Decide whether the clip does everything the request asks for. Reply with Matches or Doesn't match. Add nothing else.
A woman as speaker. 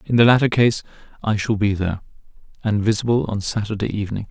Doesn't match